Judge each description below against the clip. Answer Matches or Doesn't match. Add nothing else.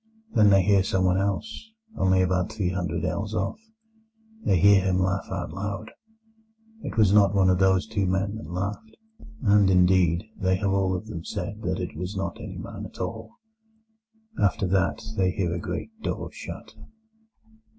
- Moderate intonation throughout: Doesn't match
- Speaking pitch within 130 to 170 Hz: Doesn't match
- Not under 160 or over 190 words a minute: Matches